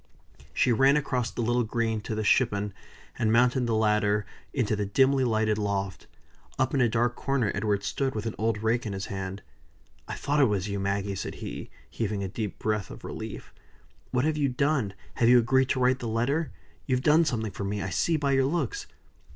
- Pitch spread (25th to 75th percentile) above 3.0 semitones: Yes, average, 4.1 semitones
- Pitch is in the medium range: No, low, 115 Hz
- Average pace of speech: No, fast, 210 wpm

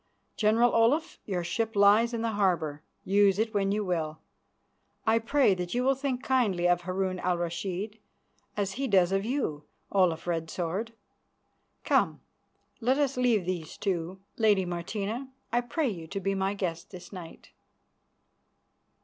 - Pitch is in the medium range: No, high, 195 Hz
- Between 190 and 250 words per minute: No, average, 155 wpm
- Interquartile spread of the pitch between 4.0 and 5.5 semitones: Yes, average, 4.5 semitones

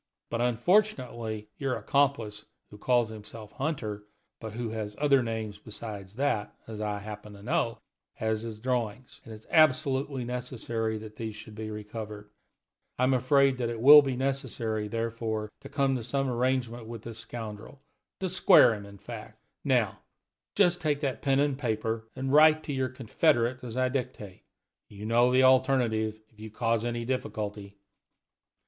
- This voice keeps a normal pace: Yes, average, 165 wpm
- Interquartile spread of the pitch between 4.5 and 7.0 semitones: No, average, 3.5 semitones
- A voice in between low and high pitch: No, low, 115 Hz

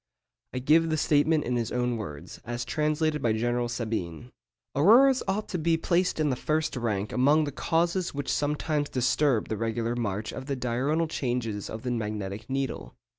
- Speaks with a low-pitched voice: Yes, low, 130 Hz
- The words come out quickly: No, average, 175 wpm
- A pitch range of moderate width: Yes, average, 5.0 semitones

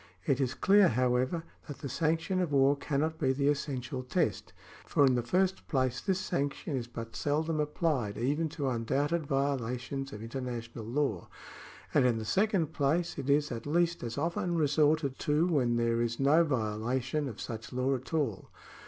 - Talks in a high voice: No, medium, 140 Hz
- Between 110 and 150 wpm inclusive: No, average, 175 wpm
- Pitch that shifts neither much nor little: Yes, average, 4.0 semitones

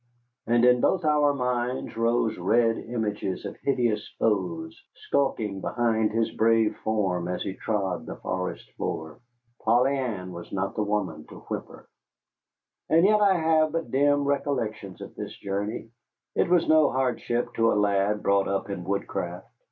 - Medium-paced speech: Yes, average, 155 wpm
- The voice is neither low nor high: No, low, 115 Hz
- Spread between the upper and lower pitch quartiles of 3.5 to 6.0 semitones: Yes, average, 5.1 semitones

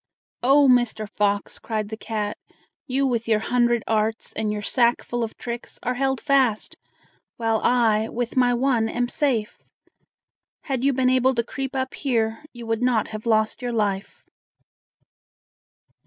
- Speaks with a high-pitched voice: Yes, high, 235 Hz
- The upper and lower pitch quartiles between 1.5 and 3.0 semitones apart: Yes, narrow, 2.6 semitones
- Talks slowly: No, average, 155 wpm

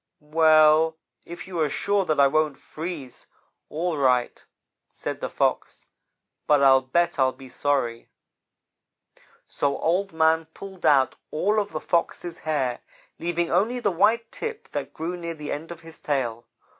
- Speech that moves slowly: No, average, 155 wpm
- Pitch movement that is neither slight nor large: Yes, average, 3.4 semitones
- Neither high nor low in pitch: Yes, medium, 160 Hz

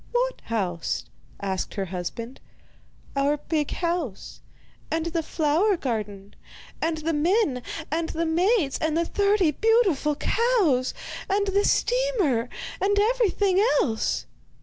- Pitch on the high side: Yes, very high, 325 Hz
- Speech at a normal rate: No, slow, 120 wpm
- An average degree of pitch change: No, wide, 7.5 semitones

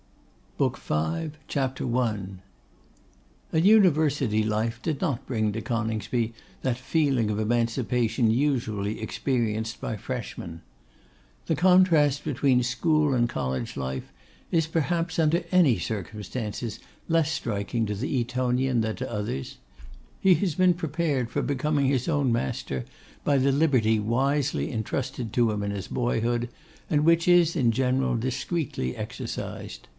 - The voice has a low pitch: Yes, low, 125 Hz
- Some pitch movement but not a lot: Yes, average, 4.9 semitones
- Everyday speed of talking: No, slow, 130 wpm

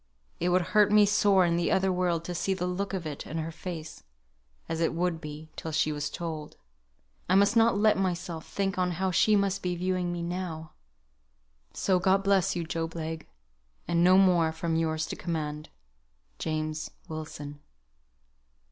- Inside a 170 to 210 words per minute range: Yes, average, 175 wpm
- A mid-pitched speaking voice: Yes, medium, 175 Hz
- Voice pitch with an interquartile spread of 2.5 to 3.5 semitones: Yes, average, 2.8 semitones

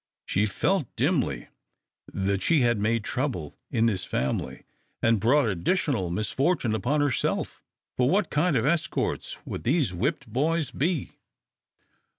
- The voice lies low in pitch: Yes, low, 125 Hz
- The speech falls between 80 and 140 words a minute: Yes, slow, 135 wpm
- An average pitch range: No, wide, 6.1 semitones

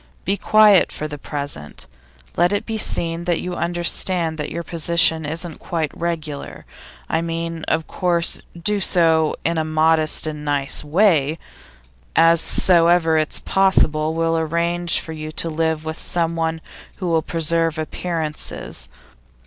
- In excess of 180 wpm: No, average, 150 wpm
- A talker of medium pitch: Yes, medium, 165 Hz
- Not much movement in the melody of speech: Yes, narrow, 1.6 semitones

